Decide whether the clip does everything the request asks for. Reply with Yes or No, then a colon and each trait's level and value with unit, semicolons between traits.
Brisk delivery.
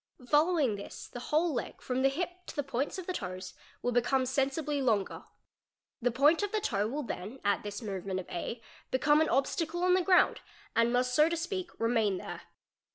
Yes: fast, 210 wpm